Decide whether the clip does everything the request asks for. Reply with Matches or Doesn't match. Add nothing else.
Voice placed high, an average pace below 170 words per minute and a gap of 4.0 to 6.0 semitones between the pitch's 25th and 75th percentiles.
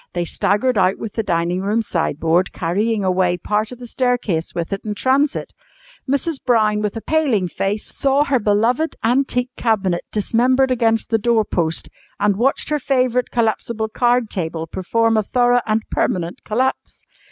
Matches